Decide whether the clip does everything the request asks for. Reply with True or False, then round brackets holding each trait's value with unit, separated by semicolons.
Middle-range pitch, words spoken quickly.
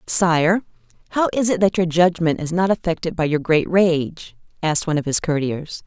False (170 Hz; 195 wpm)